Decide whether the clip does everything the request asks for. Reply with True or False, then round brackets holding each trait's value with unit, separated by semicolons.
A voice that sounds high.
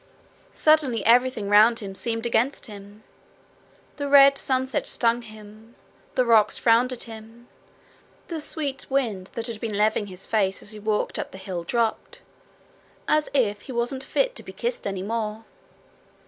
True (230 Hz)